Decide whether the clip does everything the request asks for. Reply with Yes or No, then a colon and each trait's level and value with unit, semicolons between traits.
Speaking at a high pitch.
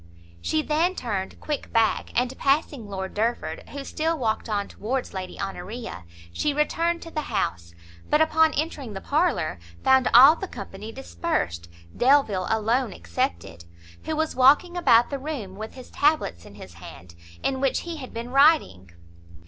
Yes: high, 245 Hz